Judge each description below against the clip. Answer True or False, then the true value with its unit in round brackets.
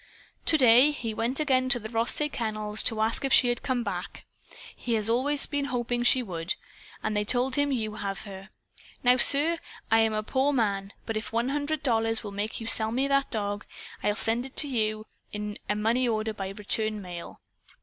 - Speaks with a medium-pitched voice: False (225 Hz)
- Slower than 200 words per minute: False (205 wpm)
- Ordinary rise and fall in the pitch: True (3.3 semitones)